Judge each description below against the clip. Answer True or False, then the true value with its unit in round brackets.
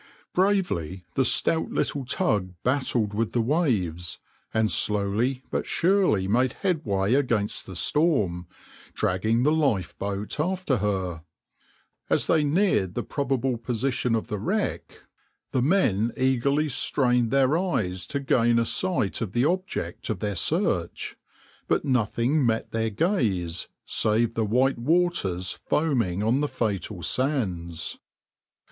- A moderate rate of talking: False (130 wpm)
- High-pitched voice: False (120 Hz)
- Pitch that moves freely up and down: True (6.1 semitones)